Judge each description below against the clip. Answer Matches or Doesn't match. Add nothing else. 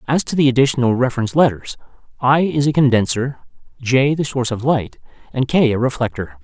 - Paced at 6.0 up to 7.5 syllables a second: Matches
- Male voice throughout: Matches